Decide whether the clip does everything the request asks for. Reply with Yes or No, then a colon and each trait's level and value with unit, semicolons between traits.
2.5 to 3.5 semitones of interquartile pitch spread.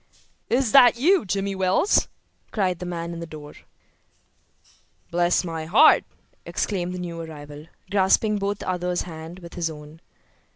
Yes: average, 3.2 semitones